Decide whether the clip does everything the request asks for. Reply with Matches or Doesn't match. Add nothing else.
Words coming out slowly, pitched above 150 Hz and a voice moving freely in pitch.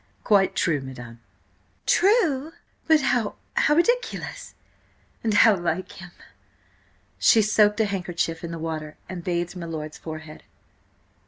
Matches